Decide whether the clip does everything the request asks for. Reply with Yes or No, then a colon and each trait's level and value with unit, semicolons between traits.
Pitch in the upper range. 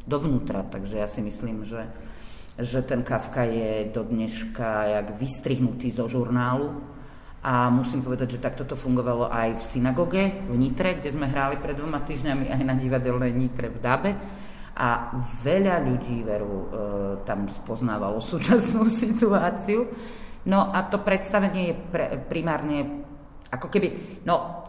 No: low, 130 Hz